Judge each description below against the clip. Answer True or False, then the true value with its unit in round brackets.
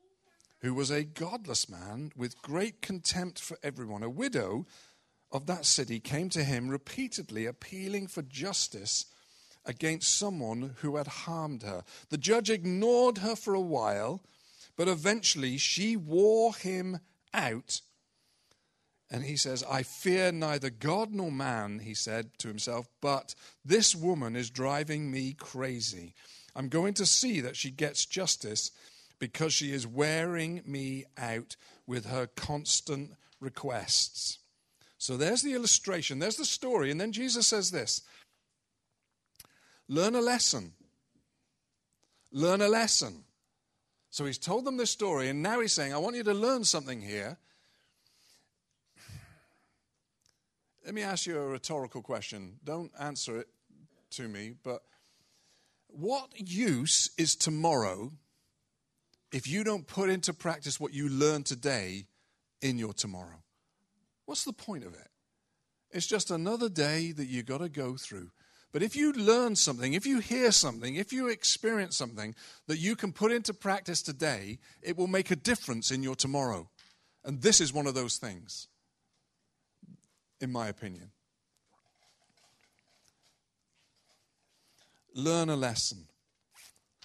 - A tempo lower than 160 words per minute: True (140 wpm)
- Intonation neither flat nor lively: False (7.0 semitones)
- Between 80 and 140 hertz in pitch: False (150 Hz)